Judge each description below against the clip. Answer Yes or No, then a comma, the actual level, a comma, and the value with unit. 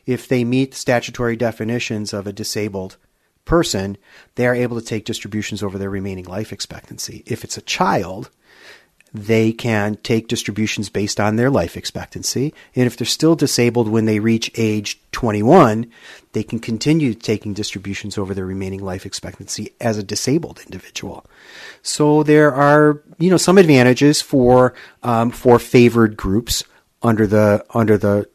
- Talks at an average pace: Yes, average, 155 wpm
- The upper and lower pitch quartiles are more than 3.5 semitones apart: No, average, 3.2 semitones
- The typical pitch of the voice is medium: No, low, 115 Hz